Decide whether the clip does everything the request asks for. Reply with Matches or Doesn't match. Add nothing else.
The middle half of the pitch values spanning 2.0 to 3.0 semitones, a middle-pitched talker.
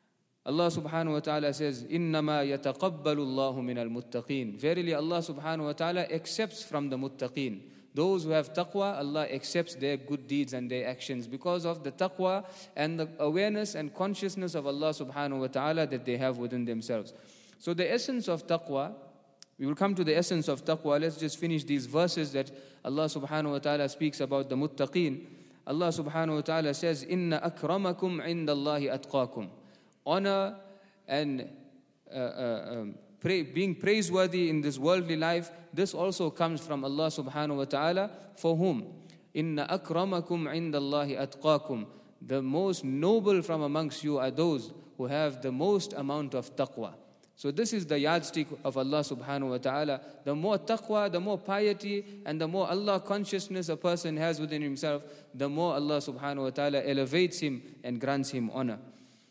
Doesn't match